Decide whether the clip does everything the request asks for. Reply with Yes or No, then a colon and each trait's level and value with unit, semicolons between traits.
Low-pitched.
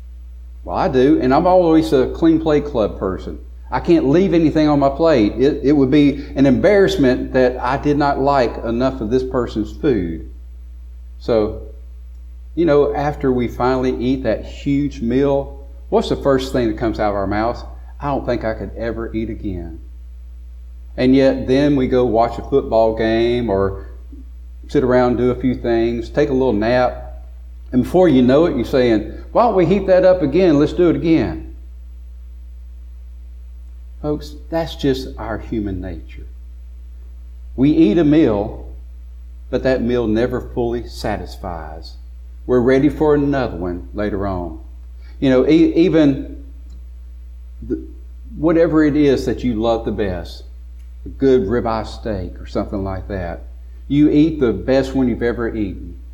Yes: low, 110 Hz